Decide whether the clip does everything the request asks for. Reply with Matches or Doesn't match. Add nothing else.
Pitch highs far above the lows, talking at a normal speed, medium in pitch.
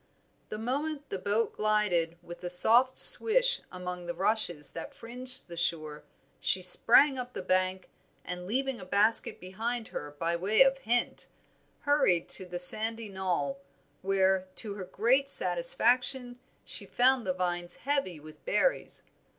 Doesn't match